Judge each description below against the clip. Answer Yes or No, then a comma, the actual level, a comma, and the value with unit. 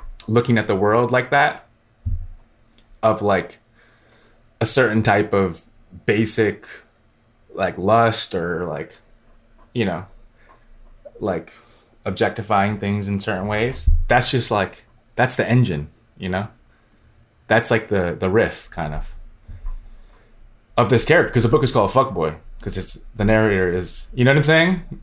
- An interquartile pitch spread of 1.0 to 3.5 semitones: Yes, average, 2.9 semitones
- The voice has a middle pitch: No, low, 110 Hz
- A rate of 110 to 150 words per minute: Yes, average, 140 wpm